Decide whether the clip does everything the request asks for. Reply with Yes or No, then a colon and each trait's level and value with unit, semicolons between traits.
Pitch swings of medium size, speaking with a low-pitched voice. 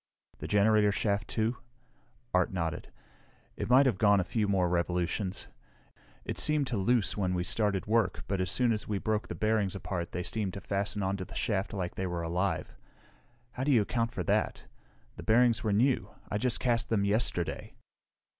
Yes: average, 3.4 semitones; low, 100 Hz